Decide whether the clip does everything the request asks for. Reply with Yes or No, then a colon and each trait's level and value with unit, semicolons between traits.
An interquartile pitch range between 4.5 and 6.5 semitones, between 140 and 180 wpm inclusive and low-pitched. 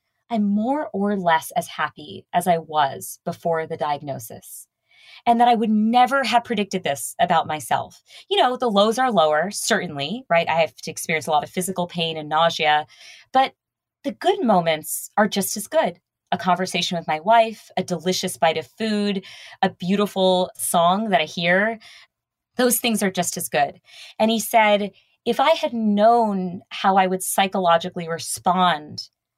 No: average, 4.9 semitones; average, 170 wpm; high, 190 Hz